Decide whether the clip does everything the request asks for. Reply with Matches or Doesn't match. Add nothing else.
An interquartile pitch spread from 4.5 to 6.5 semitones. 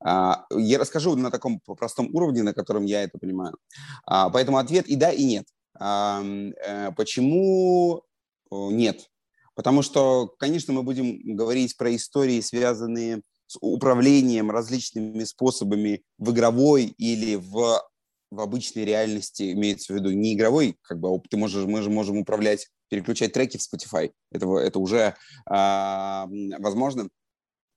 Doesn't match